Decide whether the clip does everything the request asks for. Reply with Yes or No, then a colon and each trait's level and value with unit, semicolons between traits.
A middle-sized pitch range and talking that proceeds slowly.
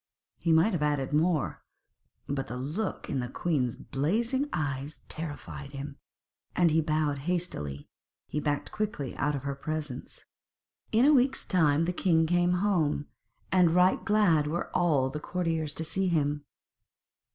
No: average, 3.8 semitones; average, 150 wpm